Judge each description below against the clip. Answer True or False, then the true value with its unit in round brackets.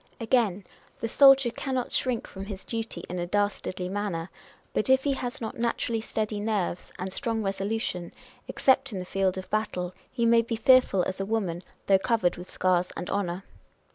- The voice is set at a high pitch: True (205 Hz)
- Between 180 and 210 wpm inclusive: True (185 wpm)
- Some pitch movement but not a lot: True (3.8 semitones)